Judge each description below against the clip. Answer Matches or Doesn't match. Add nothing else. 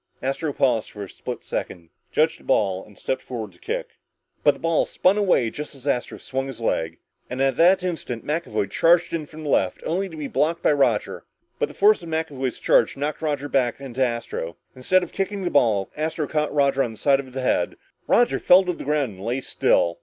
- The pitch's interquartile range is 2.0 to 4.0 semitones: Doesn't match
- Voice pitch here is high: Doesn't match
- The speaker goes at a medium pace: Doesn't match